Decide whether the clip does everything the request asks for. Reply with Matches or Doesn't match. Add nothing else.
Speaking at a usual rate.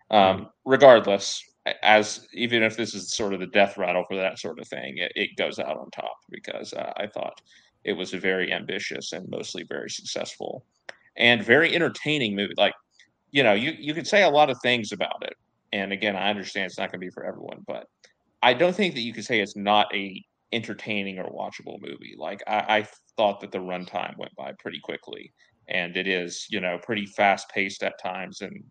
Doesn't match